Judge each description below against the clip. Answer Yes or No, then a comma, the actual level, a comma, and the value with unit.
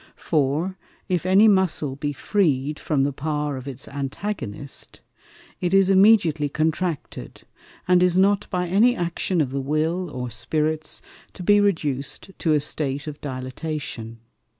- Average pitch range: Yes, average, 4.8 semitones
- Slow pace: No, average, 145 wpm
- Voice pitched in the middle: Yes, medium, 155 Hz